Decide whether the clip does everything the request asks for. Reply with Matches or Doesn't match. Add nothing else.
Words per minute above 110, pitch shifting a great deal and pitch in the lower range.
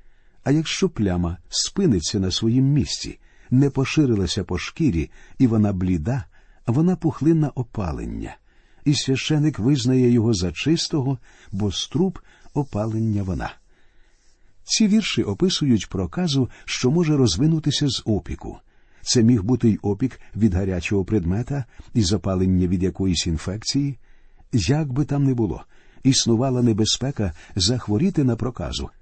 Matches